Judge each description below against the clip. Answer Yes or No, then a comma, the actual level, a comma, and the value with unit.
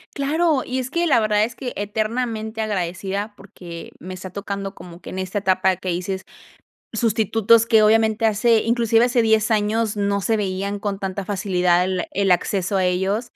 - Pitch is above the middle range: Yes, high, 205 Hz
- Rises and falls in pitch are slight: No, average, 3.0 semitones